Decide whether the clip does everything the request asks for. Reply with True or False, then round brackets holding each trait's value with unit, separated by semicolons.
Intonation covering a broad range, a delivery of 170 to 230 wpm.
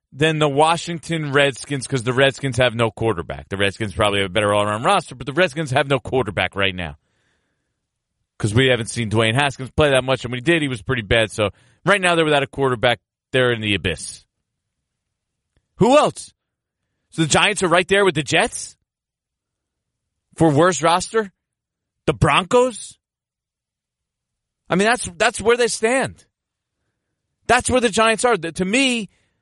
True (7.3 semitones; 175 wpm)